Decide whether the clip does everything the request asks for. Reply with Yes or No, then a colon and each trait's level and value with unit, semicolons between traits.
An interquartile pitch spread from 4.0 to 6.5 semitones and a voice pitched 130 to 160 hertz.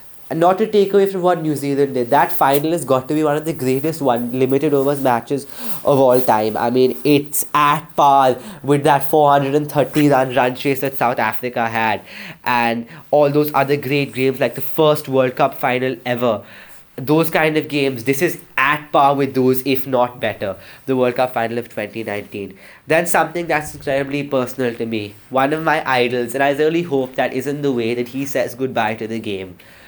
No: average, 3.2 semitones; low, 135 Hz